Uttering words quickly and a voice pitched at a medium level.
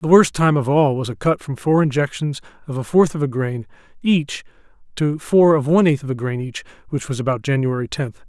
Yes: fast, 230 wpm; medium, 145 Hz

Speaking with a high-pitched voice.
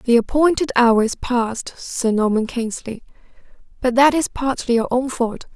Yes: high, 245 Hz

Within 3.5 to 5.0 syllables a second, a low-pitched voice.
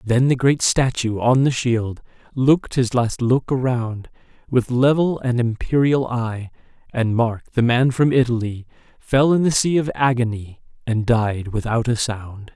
Yes: 4.2 syllables/s; low, 120 Hz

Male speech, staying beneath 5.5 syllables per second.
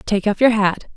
No: female; 5.3 syllables/s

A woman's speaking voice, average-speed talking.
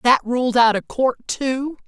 Yes: female; average, 190 wpm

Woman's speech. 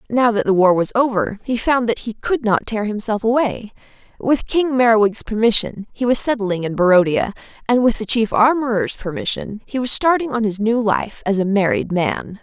Yes: female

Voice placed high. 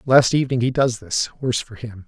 No: low, 120 Hz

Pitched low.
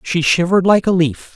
No: medium, 175 Hz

